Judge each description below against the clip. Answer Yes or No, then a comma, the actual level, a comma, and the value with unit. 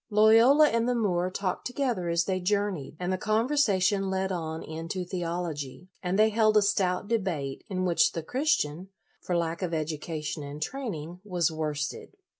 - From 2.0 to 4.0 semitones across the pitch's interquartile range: No, average, 4.4 semitones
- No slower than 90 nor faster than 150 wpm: No, average, 175 wpm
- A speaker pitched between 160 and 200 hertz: Yes, medium, 185 Hz